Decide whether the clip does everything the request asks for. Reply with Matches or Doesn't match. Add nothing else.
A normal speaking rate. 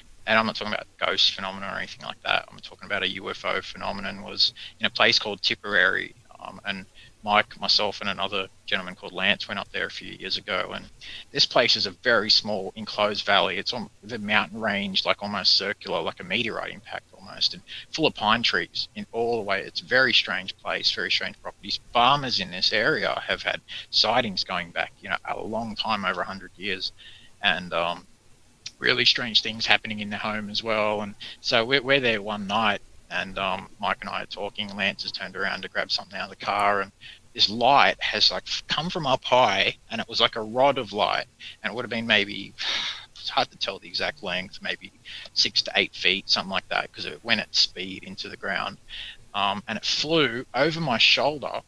Doesn't match